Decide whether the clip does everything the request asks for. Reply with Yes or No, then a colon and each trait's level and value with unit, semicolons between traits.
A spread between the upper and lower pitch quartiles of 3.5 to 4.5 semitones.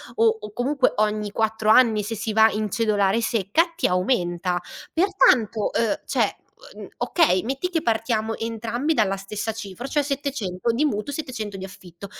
Yes: average, 4.0 semitones